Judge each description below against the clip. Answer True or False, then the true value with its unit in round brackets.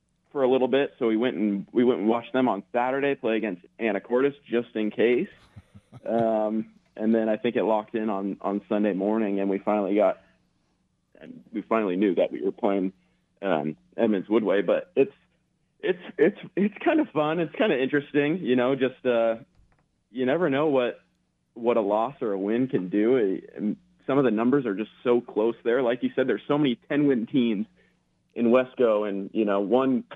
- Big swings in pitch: False (4.1 semitones)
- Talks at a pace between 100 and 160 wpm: False (200 wpm)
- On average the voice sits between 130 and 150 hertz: False (115 Hz)